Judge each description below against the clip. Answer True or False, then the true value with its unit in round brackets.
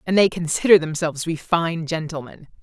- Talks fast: False (185 wpm)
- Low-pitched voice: False (165 Hz)